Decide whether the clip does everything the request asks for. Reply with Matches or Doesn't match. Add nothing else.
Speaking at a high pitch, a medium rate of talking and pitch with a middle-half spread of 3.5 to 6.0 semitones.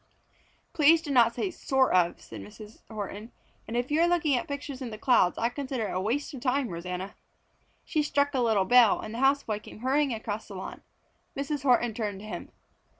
Doesn't match